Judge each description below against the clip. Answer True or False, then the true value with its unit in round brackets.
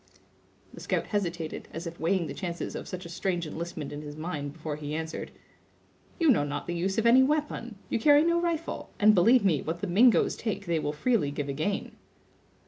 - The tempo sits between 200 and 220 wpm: True (205 wpm)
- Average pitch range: False (6.3 semitones)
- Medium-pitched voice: True (175 Hz)